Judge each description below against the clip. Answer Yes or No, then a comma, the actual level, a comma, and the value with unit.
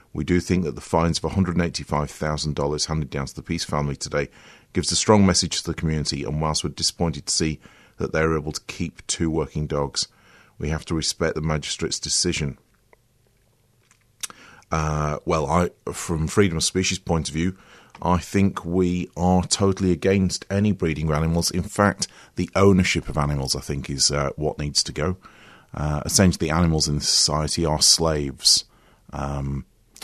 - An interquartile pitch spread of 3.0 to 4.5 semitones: Yes, average, 3.3 semitones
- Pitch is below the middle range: Yes, very low, 80 Hz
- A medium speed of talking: Yes, average, 170 wpm